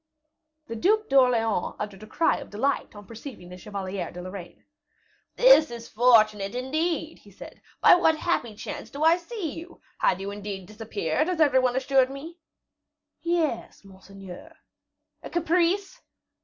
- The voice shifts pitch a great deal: Yes, wide, 8.2 semitones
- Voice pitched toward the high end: Yes, very high, 250 Hz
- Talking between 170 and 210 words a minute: No, average, 150 wpm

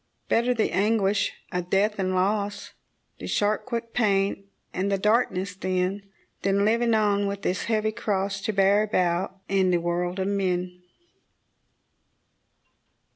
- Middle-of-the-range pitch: No, high, 200 Hz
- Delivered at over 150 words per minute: No, slow, 135 wpm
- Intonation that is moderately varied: No, narrow, 2.2 semitones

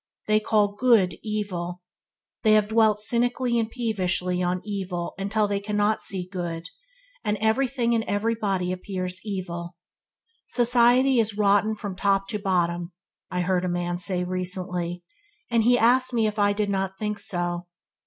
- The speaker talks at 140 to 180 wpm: Yes, average, 155 wpm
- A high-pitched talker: Yes, high, 205 Hz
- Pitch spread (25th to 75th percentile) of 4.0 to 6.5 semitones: No, average, 3.4 semitones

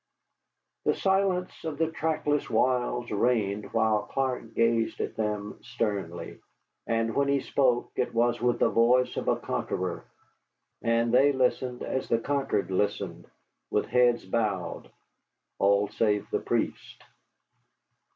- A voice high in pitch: No, low, 115 Hz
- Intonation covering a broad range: No, average, 3.8 semitones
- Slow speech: Yes, slow, 130 wpm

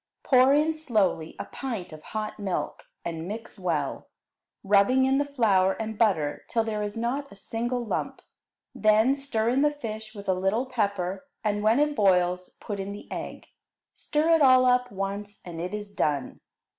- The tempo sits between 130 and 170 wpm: No, average, 180 wpm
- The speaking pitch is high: Yes, high, 215 Hz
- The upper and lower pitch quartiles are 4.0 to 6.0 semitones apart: Yes, average, 4.8 semitones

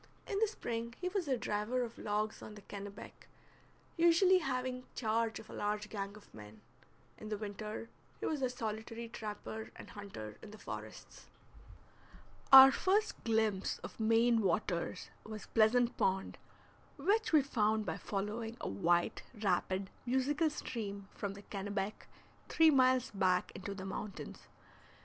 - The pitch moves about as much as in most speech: Yes, average, 3.9 semitones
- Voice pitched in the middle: No, high, 220 Hz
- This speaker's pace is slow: No, average, 150 wpm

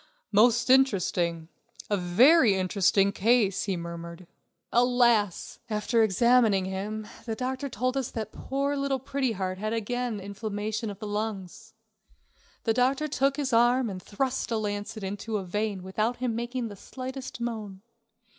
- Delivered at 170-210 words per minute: No, average, 145 wpm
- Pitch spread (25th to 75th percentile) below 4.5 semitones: Yes, average, 3.9 semitones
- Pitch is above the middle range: Yes, high, 220 Hz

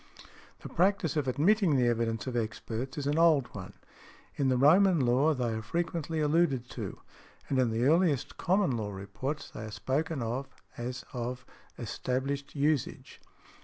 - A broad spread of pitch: No, average, 4.6 semitones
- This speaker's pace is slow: No, average, 160 wpm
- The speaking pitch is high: No, low, 135 Hz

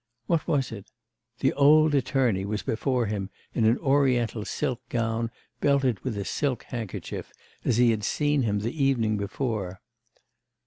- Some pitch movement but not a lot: Yes, average, 4.2 semitones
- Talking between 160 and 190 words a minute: No, average, 150 wpm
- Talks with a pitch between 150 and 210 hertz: No, low, 120 Hz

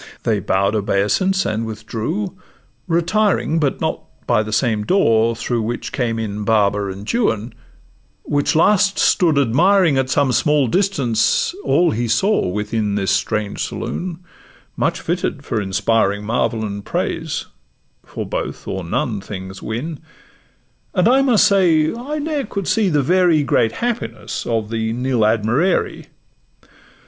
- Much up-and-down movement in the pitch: Yes, wide, 8.7 semitones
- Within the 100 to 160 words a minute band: Yes, average, 140 wpm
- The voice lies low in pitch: Yes, low, 120 Hz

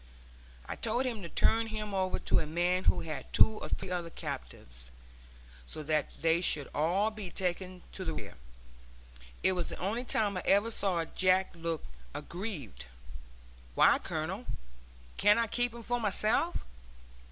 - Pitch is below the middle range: No, medium, 185 Hz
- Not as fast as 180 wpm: Yes, average, 160 wpm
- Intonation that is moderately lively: Yes, average, 4.5 semitones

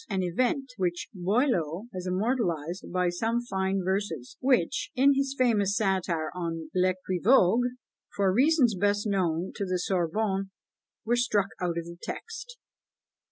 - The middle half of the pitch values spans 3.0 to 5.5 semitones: Yes, average, 5.1 semitones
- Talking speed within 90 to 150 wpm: Yes, slow, 135 wpm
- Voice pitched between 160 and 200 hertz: Yes, high, 190 Hz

